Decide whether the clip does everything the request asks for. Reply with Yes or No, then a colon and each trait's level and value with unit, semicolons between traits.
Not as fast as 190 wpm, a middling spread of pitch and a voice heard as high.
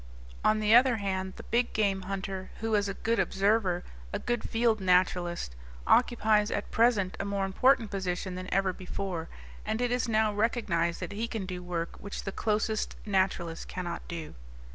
Yes: average, 175 wpm; average, 3.1 semitones; high, 200 Hz